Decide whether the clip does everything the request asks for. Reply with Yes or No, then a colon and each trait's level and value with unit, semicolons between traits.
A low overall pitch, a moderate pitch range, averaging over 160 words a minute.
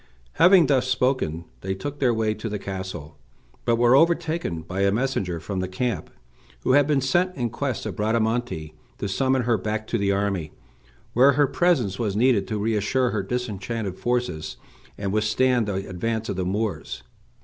Yes: low, 110 Hz; average, 4.8 semitones; average, 175 wpm